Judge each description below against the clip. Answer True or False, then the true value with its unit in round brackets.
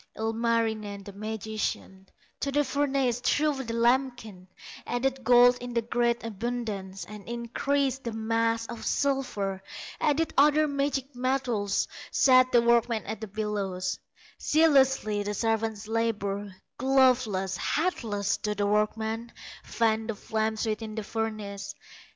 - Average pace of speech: False (120 wpm)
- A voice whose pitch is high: True (230 Hz)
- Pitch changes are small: False (3.3 semitones)